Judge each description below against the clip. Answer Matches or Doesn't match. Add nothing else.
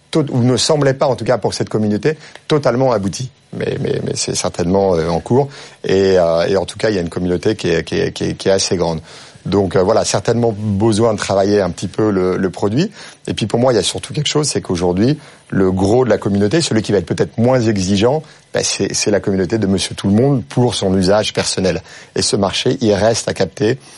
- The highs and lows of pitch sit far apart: Doesn't match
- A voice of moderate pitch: Doesn't match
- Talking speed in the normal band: Doesn't match